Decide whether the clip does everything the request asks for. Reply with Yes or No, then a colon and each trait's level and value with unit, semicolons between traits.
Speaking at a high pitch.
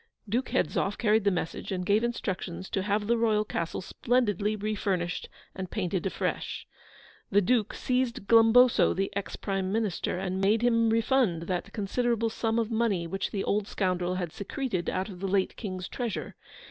Yes: high, 205 Hz